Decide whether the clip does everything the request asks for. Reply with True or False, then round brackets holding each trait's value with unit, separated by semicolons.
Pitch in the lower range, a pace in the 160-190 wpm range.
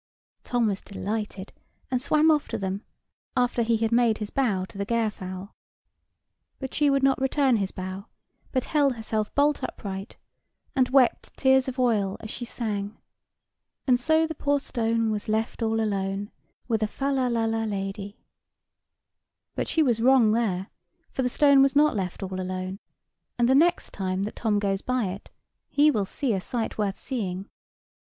False (225 Hz; 175 wpm)